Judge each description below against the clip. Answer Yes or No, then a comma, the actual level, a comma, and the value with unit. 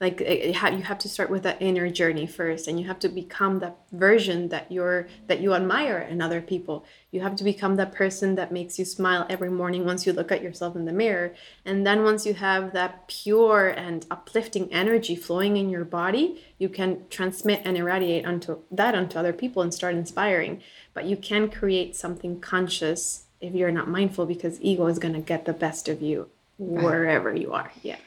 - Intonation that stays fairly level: Yes, narrow, 2.1 semitones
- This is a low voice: No, medium, 180 Hz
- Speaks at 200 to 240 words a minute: Yes, fast, 205 wpm